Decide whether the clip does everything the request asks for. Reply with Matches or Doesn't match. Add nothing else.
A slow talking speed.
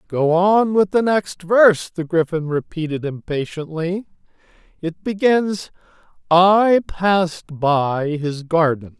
Matches